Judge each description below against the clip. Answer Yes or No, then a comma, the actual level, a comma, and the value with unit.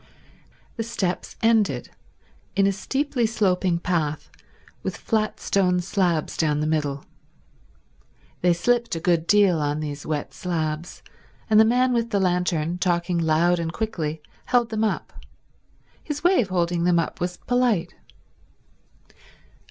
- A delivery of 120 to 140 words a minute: Yes, slow, 135 wpm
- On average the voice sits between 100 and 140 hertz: No, medium, 180 Hz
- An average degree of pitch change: Yes, average, 5.0 semitones